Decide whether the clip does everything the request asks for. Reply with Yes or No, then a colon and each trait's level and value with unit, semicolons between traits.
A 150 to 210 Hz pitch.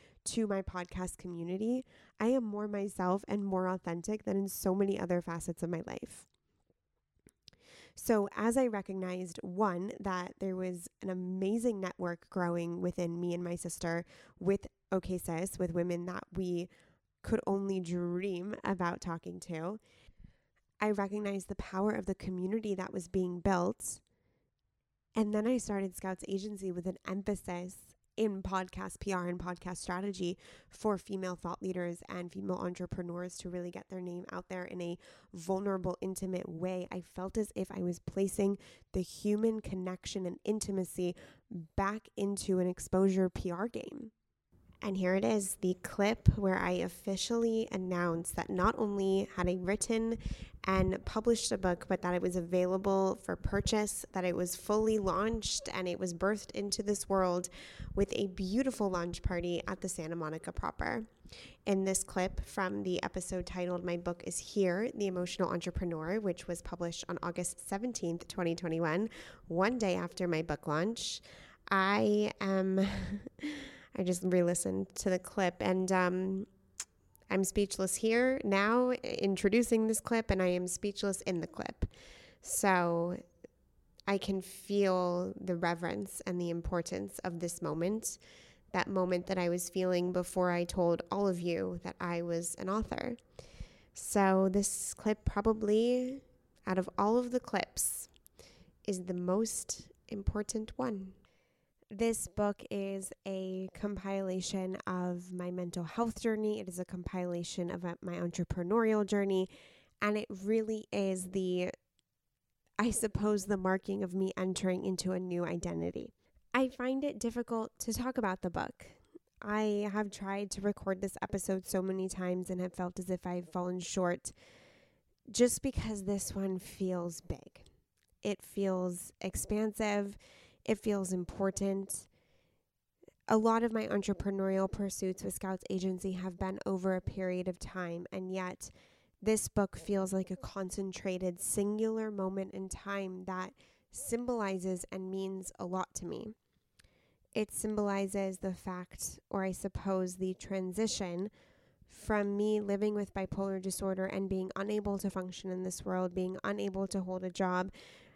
Yes: high, 190 Hz